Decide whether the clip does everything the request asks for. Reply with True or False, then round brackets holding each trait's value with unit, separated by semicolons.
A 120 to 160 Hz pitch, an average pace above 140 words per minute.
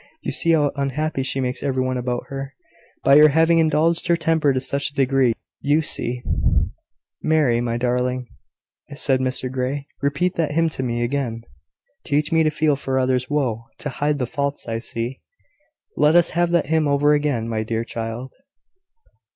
True (140 Hz; 180 wpm)